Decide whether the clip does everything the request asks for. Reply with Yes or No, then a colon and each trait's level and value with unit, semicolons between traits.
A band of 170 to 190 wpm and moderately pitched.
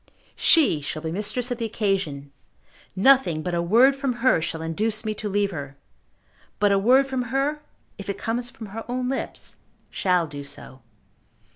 No: average, 175 wpm; high, 210 Hz